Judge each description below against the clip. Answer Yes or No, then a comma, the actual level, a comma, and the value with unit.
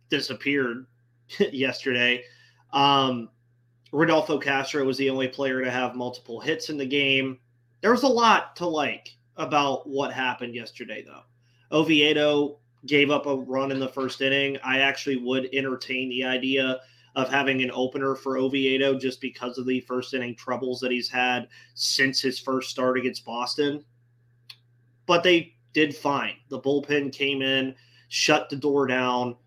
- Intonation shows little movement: Yes, narrow, 2.0 semitones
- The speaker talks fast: No, average, 155 wpm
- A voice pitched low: Yes, low, 130 Hz